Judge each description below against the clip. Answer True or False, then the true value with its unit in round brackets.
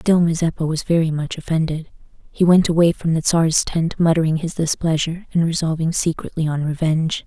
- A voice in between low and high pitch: True (165 Hz)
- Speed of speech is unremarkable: True (175 wpm)